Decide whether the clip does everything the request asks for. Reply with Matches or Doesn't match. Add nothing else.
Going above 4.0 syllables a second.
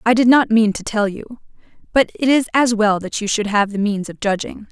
Matches